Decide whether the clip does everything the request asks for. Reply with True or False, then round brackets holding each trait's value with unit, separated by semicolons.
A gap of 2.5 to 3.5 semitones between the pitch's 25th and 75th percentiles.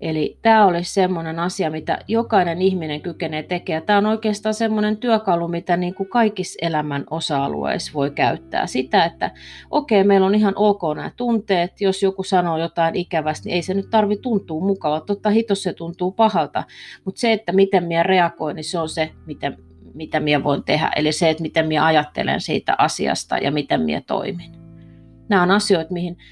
False (4.1 semitones)